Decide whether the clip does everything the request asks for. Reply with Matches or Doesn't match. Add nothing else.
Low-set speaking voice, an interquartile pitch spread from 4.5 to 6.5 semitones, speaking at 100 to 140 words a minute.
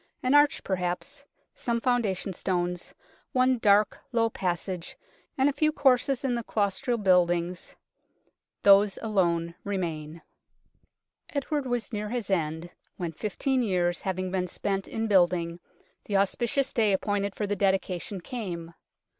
Doesn't match